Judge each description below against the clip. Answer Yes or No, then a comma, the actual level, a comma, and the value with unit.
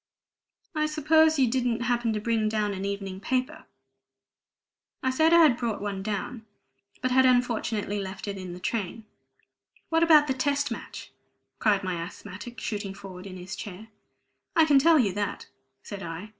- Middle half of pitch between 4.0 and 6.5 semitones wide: Yes, average, 4.9 semitones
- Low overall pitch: No, high, 220 Hz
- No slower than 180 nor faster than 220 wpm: No, average, 165 wpm